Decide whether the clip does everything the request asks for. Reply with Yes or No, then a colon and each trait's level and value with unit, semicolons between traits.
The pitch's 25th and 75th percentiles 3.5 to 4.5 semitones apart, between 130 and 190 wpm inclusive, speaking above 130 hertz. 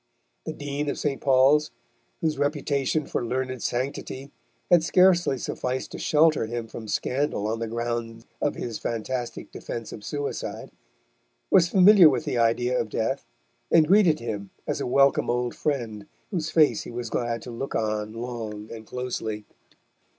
No: average, 4.1 semitones; average, 160 wpm; low, 125 Hz